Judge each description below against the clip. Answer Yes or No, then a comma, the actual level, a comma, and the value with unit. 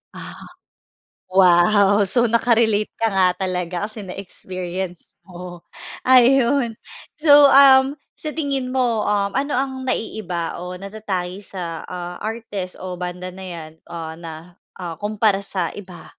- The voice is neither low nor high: No, high, 195 Hz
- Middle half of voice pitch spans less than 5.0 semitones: Yes, average, 4.6 semitones